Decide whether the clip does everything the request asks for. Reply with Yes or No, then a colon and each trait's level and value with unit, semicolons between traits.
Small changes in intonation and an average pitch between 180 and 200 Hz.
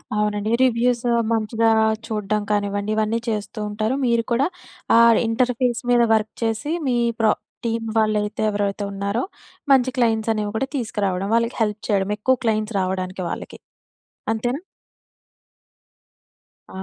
No: narrow, 2.1 semitones; high, 220 Hz